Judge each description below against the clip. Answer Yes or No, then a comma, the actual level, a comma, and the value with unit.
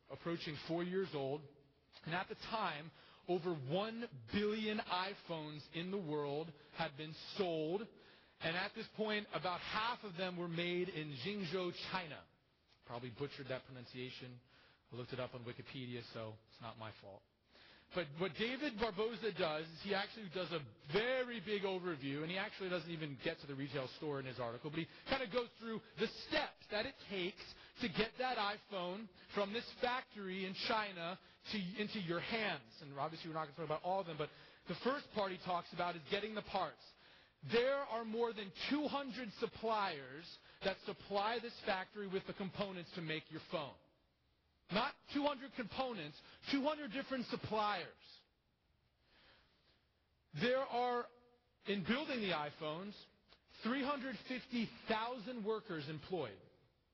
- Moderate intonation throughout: No, wide, 6.1 semitones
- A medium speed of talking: Yes, average, 160 wpm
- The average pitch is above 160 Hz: Yes, medium, 185 Hz